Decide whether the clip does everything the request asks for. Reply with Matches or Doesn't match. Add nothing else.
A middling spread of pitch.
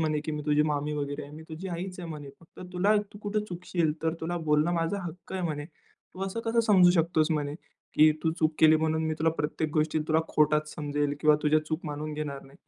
Doesn't match